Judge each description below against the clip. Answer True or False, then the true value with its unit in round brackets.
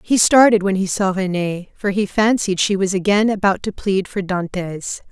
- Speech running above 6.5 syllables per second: False (4.7 syllables/s)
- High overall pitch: True (195 Hz)